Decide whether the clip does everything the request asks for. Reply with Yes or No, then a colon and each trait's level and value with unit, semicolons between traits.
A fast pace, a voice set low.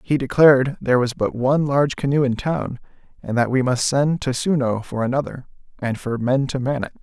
Yes: fast, 215 wpm; low, 130 Hz